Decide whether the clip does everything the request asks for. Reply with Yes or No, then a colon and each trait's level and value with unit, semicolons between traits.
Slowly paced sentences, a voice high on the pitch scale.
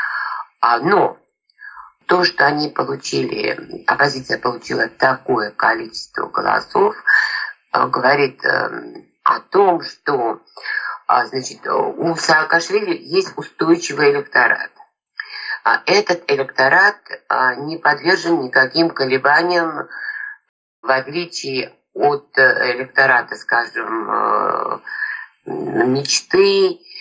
Yes: slow, 70 wpm; very high, 335 Hz